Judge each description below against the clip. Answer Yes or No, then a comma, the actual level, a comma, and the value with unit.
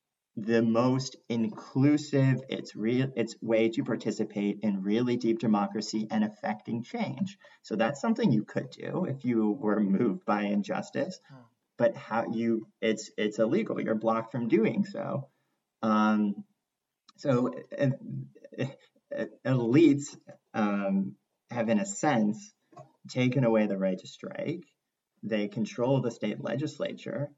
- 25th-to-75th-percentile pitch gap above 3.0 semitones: Yes, average, 4.0 semitones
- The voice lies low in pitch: Yes, low, 115 Hz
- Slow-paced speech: Yes, slow, 130 wpm